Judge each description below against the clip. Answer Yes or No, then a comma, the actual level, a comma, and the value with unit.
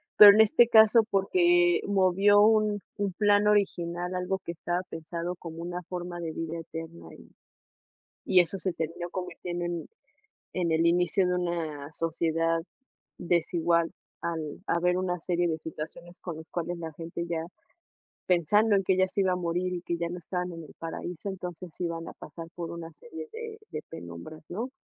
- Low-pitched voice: No, medium, 175 Hz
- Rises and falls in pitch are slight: Yes, narrow, 2.0 semitones